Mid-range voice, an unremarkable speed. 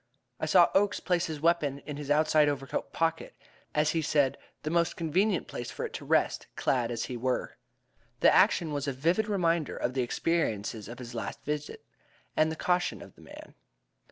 Yes: medium, 150 Hz; average, 195 wpm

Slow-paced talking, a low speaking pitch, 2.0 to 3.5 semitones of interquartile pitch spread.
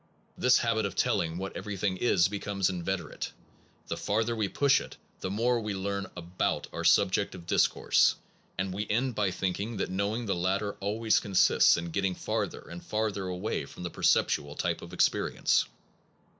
No: average, 170 wpm; low, 100 Hz; narrow, 2.5 semitones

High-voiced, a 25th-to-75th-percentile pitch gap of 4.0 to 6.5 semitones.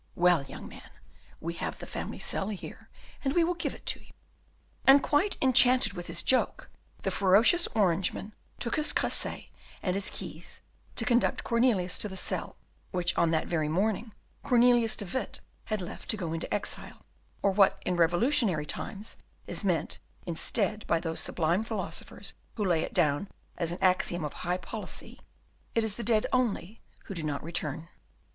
Yes: high, 195 Hz; average, 5.1 semitones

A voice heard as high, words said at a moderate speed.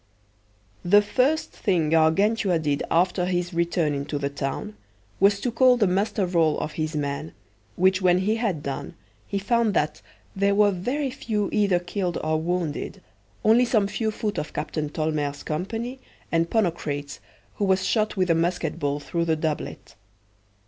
No: medium, 180 Hz; average, 160 wpm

